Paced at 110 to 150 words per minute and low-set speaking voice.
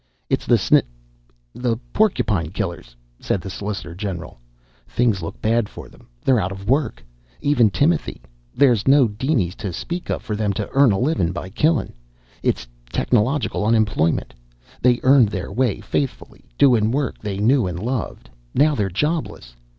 No: average, 160 wpm; low, 110 Hz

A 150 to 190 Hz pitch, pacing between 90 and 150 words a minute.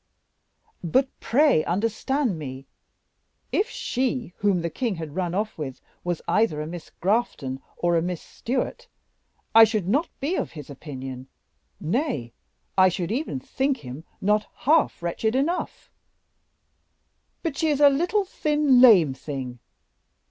No: high, 205 Hz; average, 140 wpm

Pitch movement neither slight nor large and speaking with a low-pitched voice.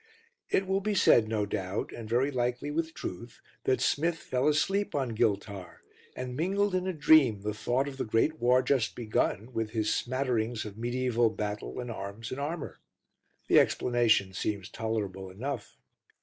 Yes: average, 4.8 semitones; low, 120 Hz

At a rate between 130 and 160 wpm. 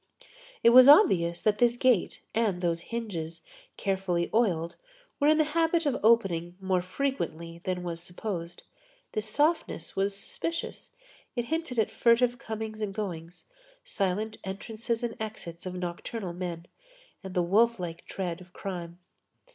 Yes: average, 145 wpm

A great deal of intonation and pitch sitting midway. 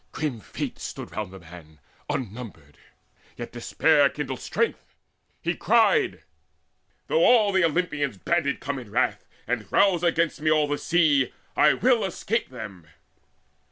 Yes: wide, 8.3 semitones; medium, 145 Hz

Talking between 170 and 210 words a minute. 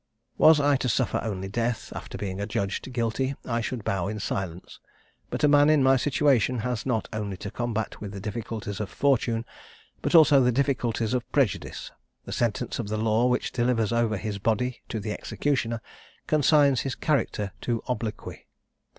Yes: average, 175 wpm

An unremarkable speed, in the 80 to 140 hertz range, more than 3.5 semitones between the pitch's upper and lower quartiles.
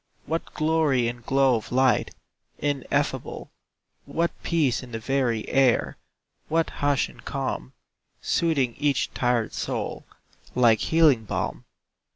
No: slow, 120 wpm; low, 135 Hz; average, 4.0 semitones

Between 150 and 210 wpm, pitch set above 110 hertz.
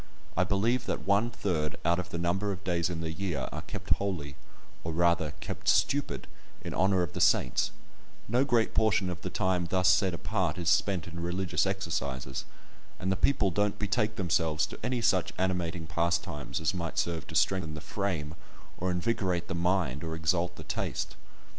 No: average, 185 wpm; very low, 90 Hz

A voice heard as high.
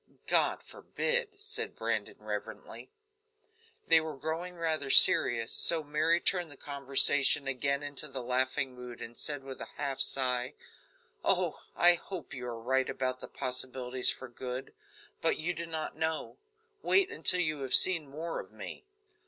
No: medium, 140 Hz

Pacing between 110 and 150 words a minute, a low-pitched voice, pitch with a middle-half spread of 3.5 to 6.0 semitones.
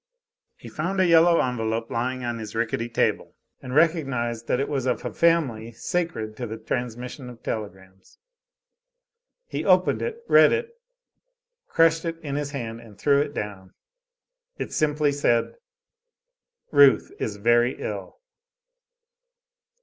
Yes: slow, 135 wpm; low, 125 Hz; average, 5.2 semitones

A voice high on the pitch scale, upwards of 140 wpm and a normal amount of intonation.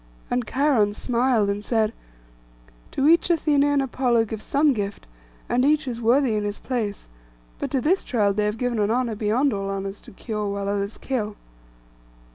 Yes: high, 230 Hz; average, 180 wpm; average, 4.3 semitones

